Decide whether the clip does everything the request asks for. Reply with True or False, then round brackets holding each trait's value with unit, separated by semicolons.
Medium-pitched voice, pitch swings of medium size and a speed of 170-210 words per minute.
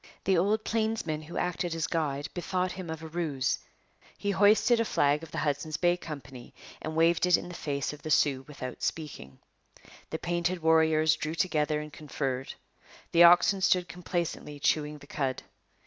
True (160 Hz; 3.0 semitones; 175 wpm)